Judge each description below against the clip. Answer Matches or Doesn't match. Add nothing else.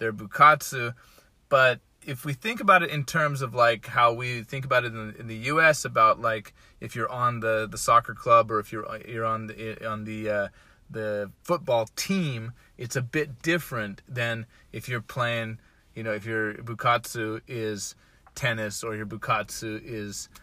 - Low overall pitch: Matches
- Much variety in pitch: Doesn't match